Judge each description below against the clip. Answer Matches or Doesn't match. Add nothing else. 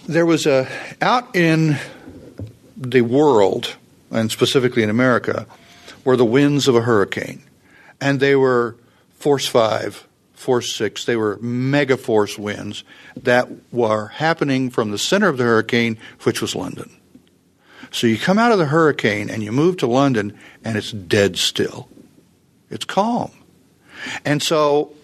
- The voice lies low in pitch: Matches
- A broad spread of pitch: Doesn't match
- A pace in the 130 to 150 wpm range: Matches